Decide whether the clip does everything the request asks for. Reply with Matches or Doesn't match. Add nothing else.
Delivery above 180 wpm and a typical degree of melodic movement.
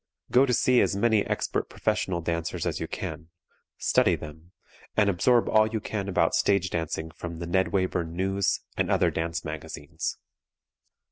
Doesn't match